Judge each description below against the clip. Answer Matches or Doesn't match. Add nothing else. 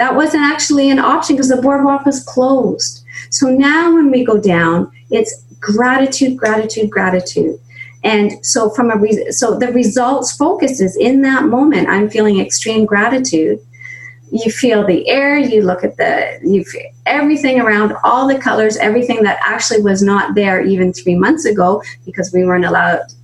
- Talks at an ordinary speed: Matches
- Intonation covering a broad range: Matches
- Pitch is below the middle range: Doesn't match